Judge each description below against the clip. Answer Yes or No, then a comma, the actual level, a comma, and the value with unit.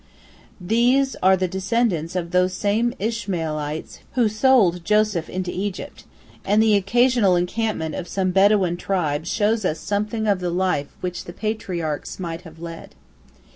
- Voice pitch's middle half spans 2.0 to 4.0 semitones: Yes, average, 3.7 semitones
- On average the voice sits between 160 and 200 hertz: Yes, high, 190 Hz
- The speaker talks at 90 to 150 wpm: Yes, average, 145 wpm